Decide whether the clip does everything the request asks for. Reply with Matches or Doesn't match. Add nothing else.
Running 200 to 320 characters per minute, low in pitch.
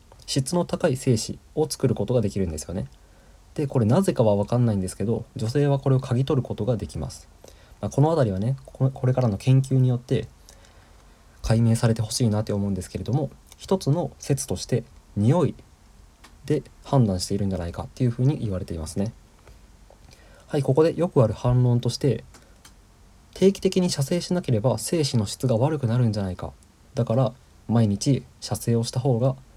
Doesn't match